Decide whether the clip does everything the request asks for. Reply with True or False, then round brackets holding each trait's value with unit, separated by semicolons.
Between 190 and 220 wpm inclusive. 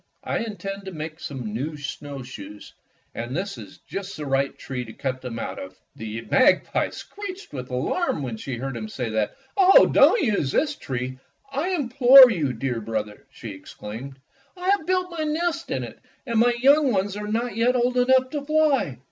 True (195 wpm)